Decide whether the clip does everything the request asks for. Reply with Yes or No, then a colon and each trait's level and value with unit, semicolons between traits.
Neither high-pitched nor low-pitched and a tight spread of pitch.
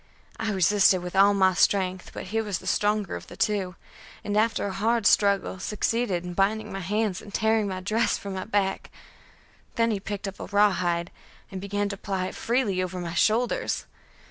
No: high, 200 Hz; narrow, 2.3 semitones